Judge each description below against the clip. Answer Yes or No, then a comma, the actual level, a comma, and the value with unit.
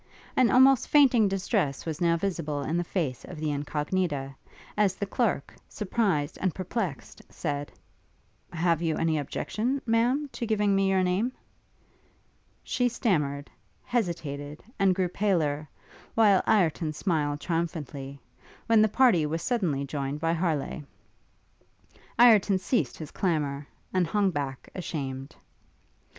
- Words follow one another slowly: Yes, slow, 130 wpm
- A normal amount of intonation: No, wide, 5.8 semitones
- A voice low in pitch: No, medium, 175 Hz